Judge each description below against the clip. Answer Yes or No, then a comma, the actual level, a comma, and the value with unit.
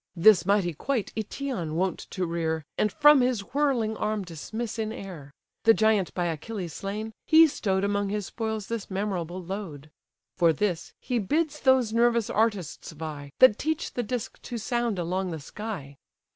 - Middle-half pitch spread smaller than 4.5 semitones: No, average, 4.9 semitones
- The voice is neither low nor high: No, high, 205 Hz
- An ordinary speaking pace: Yes, average, 165 wpm